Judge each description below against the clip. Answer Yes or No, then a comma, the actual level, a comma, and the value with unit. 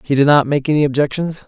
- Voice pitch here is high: No, medium, 145 Hz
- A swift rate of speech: Yes, fast, 245 wpm